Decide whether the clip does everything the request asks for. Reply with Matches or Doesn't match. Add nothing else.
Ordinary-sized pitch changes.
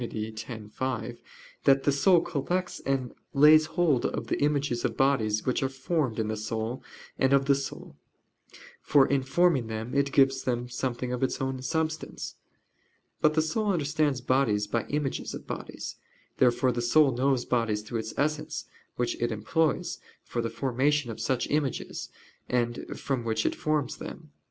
Matches